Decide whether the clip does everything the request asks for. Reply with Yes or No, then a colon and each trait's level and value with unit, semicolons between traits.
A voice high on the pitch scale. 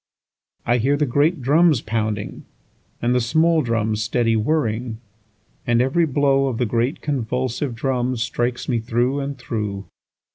No: low, 120 Hz